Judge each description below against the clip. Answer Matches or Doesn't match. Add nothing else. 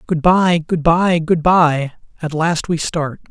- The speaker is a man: Matches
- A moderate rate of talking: Matches